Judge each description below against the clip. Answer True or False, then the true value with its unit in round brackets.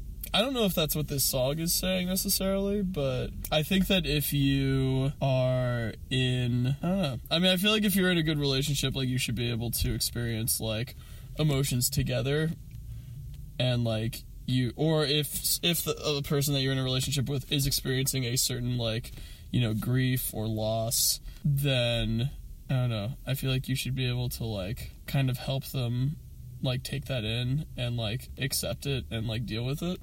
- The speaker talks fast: False (195 wpm)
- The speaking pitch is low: True (130 Hz)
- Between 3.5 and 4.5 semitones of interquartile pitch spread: False (3.1 semitones)